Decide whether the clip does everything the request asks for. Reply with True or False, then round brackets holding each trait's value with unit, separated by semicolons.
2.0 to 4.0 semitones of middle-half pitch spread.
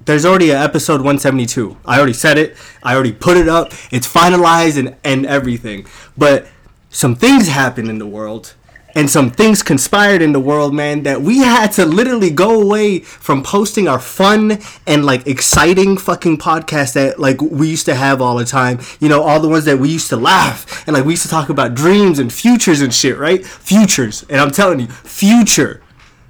False (4.9 semitones)